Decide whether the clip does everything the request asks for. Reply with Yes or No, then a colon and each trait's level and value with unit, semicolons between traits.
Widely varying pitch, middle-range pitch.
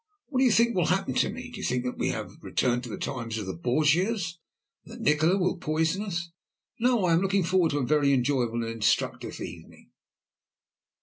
Yes: wide, 7.4 semitones; medium, 165 Hz